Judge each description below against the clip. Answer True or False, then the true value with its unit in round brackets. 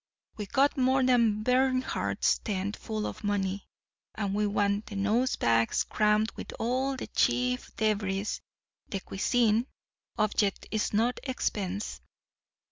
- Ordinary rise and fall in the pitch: True (3.5 semitones)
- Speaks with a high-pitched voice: True (210 Hz)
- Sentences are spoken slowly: True (125 wpm)